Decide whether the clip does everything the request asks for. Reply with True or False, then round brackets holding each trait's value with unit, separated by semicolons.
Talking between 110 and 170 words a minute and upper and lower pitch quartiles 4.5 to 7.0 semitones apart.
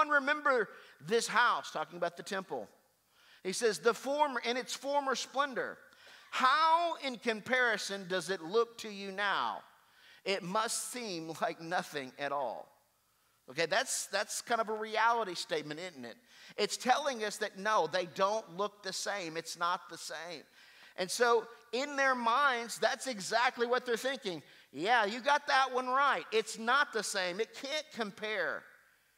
True (160 wpm; 5.2 semitones)